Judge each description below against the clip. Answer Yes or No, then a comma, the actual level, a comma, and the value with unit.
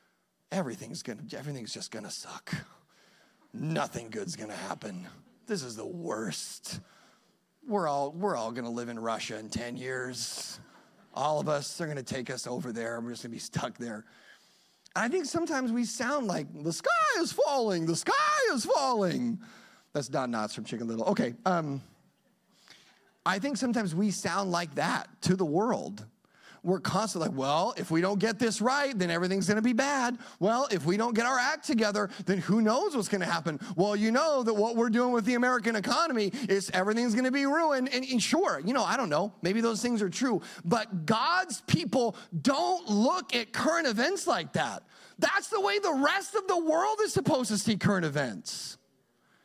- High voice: Yes, high, 215 Hz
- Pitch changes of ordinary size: No, wide, 7.2 semitones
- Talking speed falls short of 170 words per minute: No, average, 185 wpm